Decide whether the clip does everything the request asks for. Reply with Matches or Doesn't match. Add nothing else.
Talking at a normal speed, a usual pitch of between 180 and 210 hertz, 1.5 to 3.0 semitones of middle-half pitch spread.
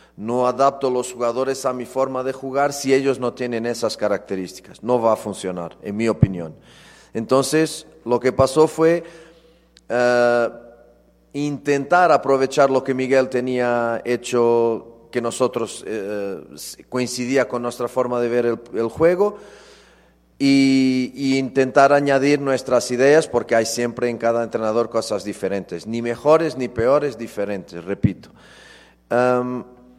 Doesn't match